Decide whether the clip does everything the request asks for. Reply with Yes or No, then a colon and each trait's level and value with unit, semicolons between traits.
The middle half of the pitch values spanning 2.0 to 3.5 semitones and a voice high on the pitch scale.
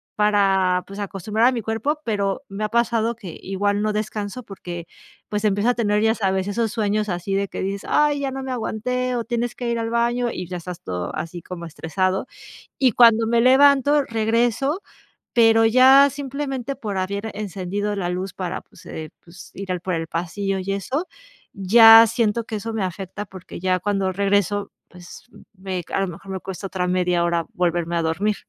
No: average, 3.9 semitones; high, 205 Hz